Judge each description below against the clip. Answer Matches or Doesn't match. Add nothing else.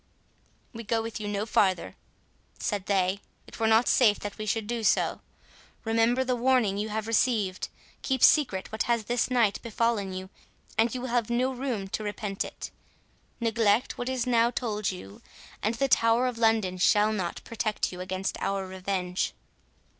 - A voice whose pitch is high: Matches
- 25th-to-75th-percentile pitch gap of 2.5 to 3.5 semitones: Matches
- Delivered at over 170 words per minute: Doesn't match